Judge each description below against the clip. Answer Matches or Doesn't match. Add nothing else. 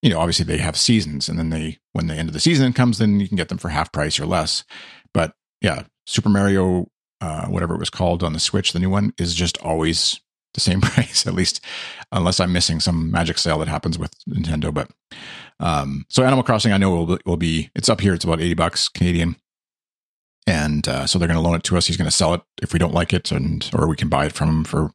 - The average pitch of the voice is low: Matches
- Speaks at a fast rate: Matches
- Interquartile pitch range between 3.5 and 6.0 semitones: Doesn't match